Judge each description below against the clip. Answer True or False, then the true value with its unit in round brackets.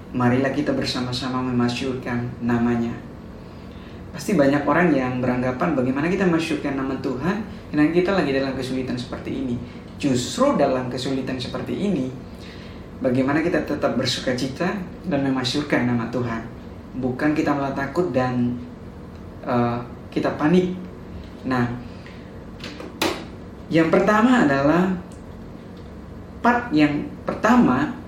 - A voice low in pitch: True (130 Hz)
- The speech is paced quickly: False (110 wpm)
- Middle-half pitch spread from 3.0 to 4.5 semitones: True (3.5 semitones)